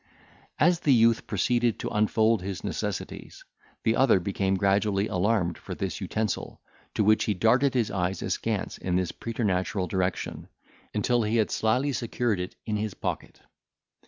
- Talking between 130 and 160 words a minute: Yes, average, 155 wpm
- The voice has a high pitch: No, low, 105 Hz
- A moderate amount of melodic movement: Yes, average, 3.2 semitones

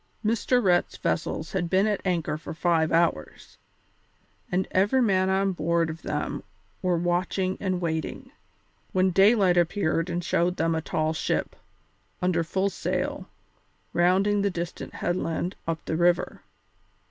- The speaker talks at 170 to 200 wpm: No, average, 140 wpm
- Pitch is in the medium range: Yes, medium, 175 Hz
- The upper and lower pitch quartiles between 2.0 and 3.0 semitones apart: Yes, narrow, 2.4 semitones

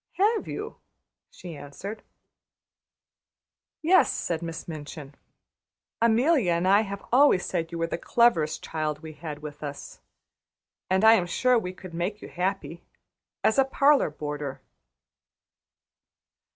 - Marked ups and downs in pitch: Yes, wide, 6.2 semitones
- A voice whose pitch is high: No, medium, 175 Hz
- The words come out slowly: Yes, slow, 130 wpm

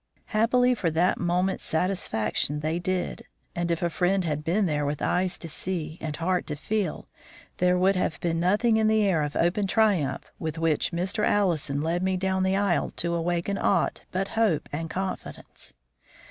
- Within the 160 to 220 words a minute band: Yes, average, 180 wpm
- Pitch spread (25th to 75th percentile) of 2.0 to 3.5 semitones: Yes, average, 3.0 semitones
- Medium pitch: Yes, medium, 180 Hz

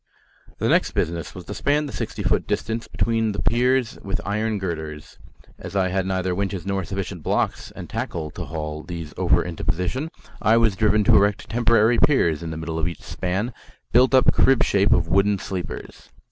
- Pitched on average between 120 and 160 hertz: No, very low, 95 Hz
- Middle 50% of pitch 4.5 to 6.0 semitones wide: Yes, average, 4.8 semitones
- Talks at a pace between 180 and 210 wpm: Yes, average, 190 wpm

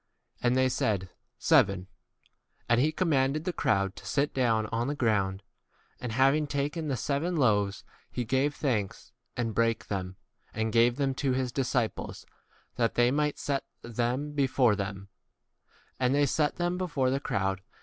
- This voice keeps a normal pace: Yes, average, 165 wpm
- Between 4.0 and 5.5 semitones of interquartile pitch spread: Yes, average, 4.4 semitones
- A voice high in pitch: No, low, 125 Hz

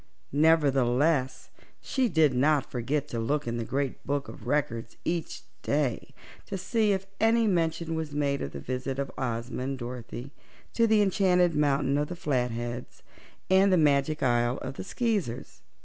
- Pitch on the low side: No, medium, 145 Hz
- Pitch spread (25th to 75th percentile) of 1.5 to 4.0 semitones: No, average, 5.0 semitones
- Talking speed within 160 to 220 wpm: Yes, average, 165 wpm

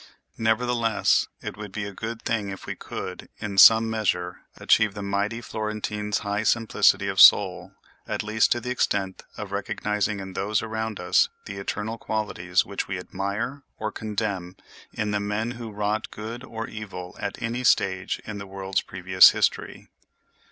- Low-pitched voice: Yes, low, 105 Hz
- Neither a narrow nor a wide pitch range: No, narrow, 2.1 semitones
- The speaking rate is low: No, average, 165 wpm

